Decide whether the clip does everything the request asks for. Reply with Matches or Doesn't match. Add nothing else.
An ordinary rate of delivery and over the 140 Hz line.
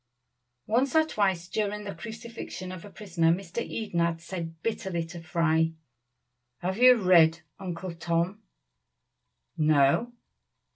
Doesn't match